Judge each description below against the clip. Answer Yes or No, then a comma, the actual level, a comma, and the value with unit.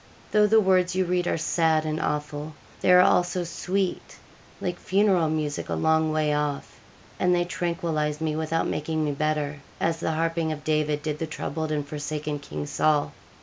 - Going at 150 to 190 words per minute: Yes, average, 180 wpm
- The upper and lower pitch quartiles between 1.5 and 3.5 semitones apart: Yes, narrow, 2.6 semitones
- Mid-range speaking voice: Yes, medium, 155 Hz